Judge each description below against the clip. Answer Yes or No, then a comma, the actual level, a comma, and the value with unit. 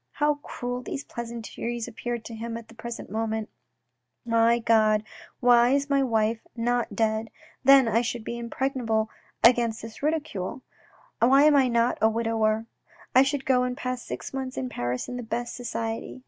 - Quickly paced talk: No, average, 170 wpm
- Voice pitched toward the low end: No, high, 235 Hz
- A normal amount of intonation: No, narrow, 2.1 semitones